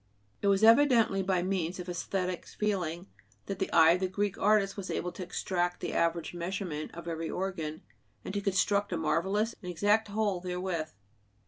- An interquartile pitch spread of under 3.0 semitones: Yes, narrow, 2.6 semitones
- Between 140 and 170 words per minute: No, average, 180 wpm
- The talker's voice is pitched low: No, medium, 185 Hz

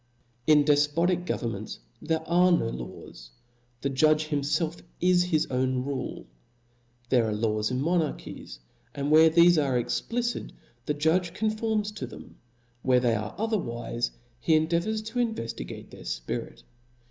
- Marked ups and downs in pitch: Yes, wide, 6.5 semitones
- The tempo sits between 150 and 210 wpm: No, average, 140 wpm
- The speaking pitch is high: No, medium, 150 Hz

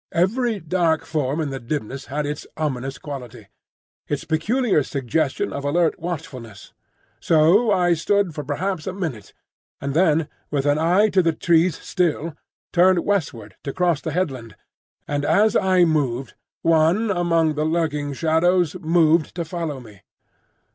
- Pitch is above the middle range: No, medium, 160 Hz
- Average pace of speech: Yes, average, 145 wpm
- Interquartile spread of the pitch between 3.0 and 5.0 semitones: Yes, average, 3.6 semitones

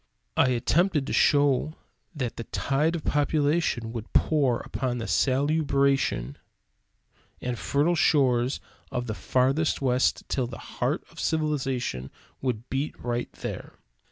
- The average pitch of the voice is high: No, low, 135 Hz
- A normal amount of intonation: Yes, average, 3.3 semitones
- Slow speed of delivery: Yes, slow, 130 wpm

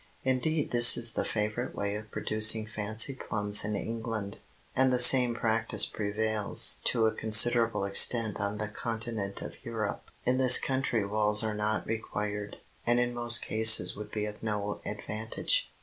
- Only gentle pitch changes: Yes, narrow, 2.2 semitones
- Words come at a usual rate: Yes, average, 160 wpm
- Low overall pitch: Yes, low, 110 Hz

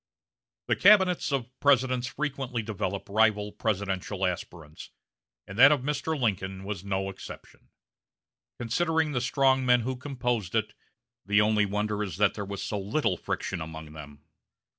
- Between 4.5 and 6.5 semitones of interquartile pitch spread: Yes, average, 5.2 semitones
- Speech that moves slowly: No, average, 145 wpm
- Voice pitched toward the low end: Yes, low, 110 Hz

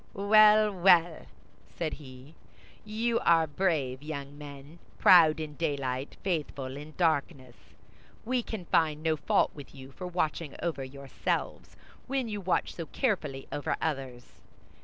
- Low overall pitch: No, medium, 155 Hz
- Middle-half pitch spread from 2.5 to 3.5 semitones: No, average, 4.7 semitones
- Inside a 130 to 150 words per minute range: Yes, slow, 135 wpm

